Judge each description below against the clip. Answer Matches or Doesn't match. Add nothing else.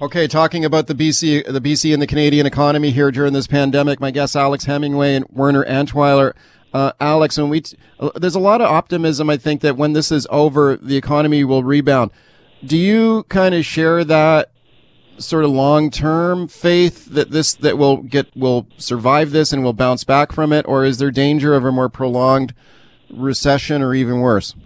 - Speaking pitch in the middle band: Matches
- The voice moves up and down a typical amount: Doesn't match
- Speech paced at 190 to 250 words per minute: Matches